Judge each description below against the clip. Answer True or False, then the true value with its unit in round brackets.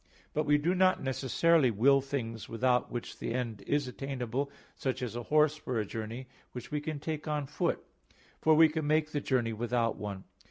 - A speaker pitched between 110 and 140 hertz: True (135 Hz)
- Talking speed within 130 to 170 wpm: False (195 wpm)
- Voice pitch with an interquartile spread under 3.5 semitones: False (4.1 semitones)